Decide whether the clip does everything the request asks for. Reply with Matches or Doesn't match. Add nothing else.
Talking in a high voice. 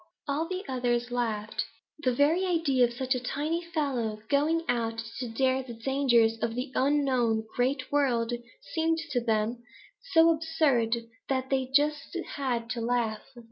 Matches